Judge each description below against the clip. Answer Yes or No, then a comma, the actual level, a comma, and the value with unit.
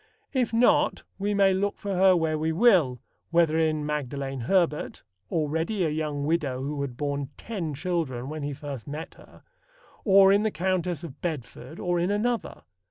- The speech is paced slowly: No, average, 170 wpm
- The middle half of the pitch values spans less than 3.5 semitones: No, average, 4.7 semitones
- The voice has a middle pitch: Yes, medium, 160 Hz